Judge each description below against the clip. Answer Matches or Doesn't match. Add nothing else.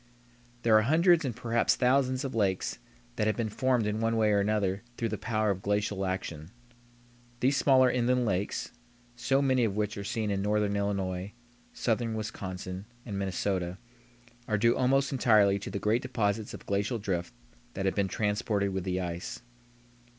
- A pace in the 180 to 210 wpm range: Doesn't match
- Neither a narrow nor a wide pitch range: Matches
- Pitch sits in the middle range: Doesn't match